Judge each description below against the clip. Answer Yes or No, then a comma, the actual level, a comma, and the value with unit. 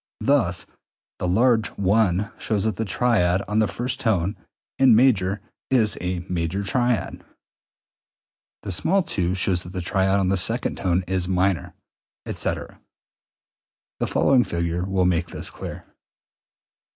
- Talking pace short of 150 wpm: Yes, average, 140 wpm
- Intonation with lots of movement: No, average, 3.8 semitones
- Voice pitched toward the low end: Yes, very low, 95 Hz